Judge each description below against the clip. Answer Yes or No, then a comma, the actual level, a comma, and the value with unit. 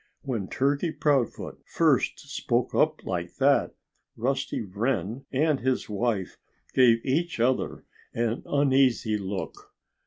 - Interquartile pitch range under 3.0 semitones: No, average, 4.0 semitones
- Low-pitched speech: Yes, low, 125 Hz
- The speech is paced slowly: Yes, slow, 115 wpm